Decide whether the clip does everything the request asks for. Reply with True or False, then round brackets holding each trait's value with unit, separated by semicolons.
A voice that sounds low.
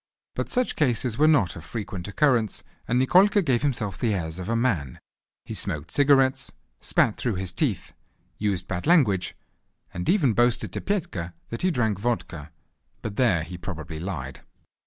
True (110 Hz)